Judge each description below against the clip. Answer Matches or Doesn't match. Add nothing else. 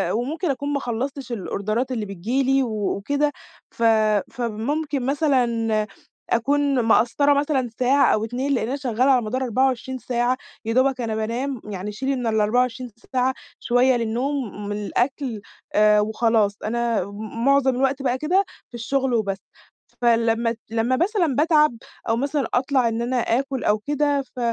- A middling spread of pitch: Matches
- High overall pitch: Matches